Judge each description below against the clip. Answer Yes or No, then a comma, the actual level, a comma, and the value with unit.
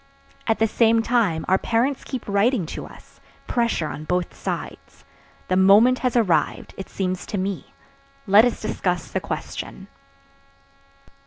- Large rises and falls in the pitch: No, average, 4.1 semitones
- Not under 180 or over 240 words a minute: No, average, 145 wpm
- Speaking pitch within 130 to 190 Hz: No, high, 205 Hz